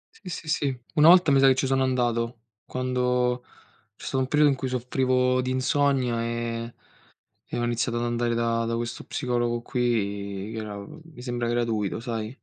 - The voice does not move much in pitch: Yes, narrow, 1.9 semitones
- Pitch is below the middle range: Yes, low, 125 Hz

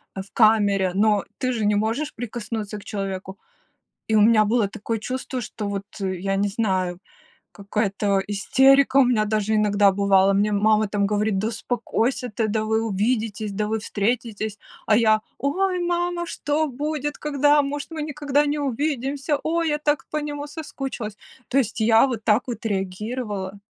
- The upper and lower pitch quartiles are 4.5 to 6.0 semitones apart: Yes, average, 5.0 semitones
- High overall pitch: Yes, high, 220 Hz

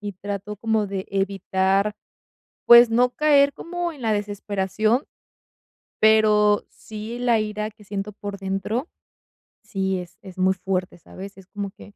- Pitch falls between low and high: No, high, 205 Hz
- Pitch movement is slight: Yes, narrow, 2.3 semitones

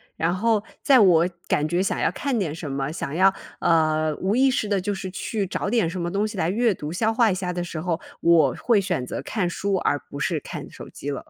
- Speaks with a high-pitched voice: No, medium, 180 Hz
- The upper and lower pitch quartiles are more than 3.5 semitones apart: Yes, average, 4.2 semitones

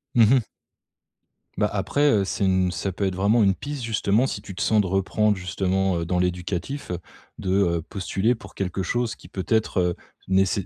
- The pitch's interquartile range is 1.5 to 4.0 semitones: Yes, average, 2.8 semitones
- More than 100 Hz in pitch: No, very low, 95 Hz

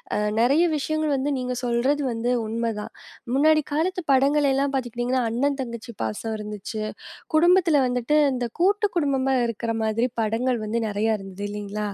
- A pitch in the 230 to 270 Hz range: Yes, very high, 250 Hz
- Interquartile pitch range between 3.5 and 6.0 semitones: Yes, average, 4.3 semitones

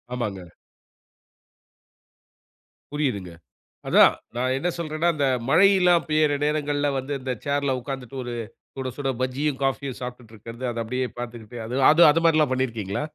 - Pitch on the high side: No, low, 130 Hz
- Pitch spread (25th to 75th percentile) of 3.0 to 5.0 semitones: Yes, average, 3.5 semitones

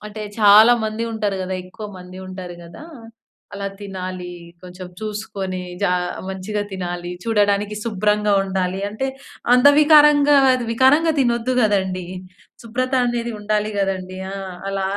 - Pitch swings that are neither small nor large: Yes, average, 3.5 semitones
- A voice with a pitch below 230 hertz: Yes, high, 205 Hz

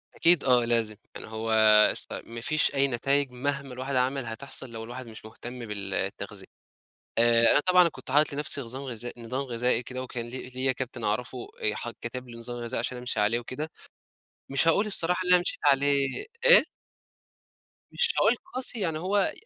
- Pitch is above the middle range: No, low, 130 Hz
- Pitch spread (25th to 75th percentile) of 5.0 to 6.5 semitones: No, average, 3.3 semitones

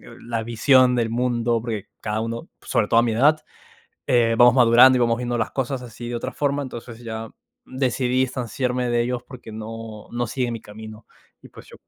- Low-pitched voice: Yes, low, 120 Hz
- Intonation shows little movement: Yes, narrow, 1.8 semitones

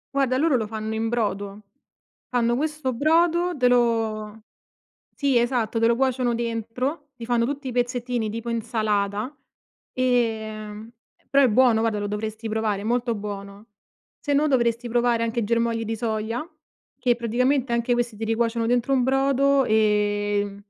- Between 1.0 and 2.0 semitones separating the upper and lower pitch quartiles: No, narrow, 2.6 semitones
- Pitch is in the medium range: No, high, 235 Hz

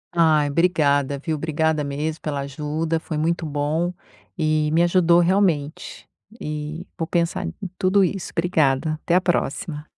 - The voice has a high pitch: No, medium, 160 Hz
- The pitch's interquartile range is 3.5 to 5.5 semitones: No, narrow, 2.6 semitones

